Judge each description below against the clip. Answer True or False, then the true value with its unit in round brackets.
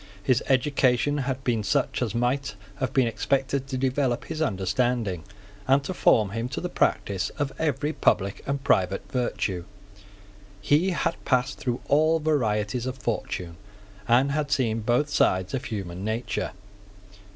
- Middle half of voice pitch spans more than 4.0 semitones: True (4.5 semitones)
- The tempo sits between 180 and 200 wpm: False (150 wpm)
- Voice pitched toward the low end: True (125 Hz)